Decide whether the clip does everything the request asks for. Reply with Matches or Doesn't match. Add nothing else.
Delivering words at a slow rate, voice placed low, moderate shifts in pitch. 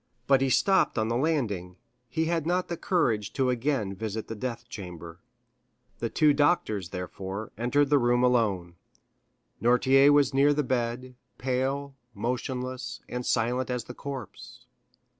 Doesn't match